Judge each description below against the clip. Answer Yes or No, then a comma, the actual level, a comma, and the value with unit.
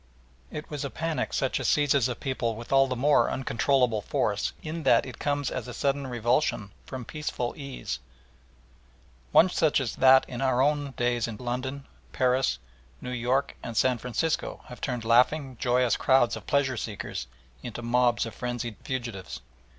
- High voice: No, low, 125 Hz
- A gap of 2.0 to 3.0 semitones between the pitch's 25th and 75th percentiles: Yes, narrow, 2.6 semitones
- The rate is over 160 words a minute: Yes, average, 170 wpm